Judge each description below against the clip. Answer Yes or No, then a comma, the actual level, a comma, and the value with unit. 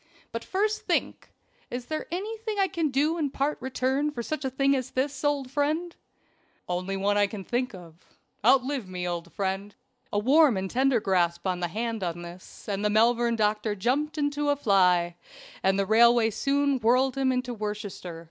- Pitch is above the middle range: Yes, high, 240 Hz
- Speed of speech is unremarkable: Yes, average, 185 wpm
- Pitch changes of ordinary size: No, wide, 6.3 semitones